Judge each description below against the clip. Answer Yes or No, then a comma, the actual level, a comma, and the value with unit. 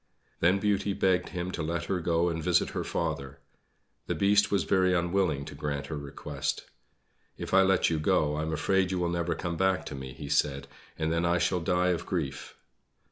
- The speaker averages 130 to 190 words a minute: No, fast, 205 wpm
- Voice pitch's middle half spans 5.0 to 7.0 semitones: No, average, 3.3 semitones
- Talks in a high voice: No, very low, 85 Hz